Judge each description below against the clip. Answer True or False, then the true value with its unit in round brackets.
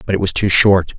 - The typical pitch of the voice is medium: False (95 Hz)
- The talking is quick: True (305 wpm)